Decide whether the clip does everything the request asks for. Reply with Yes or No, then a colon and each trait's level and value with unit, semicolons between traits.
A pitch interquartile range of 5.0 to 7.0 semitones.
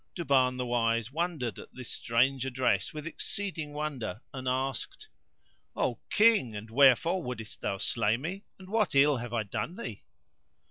Yes: average, 5.3 semitones